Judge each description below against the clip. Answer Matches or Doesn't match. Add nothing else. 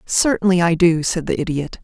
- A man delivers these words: Doesn't match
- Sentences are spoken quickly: Doesn't match